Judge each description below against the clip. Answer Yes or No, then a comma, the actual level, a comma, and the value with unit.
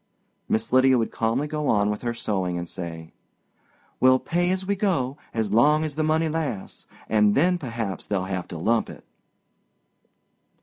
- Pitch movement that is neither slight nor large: No, wide, 7.0 semitones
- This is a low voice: Yes, low, 120 Hz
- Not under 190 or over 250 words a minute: No, average, 170 wpm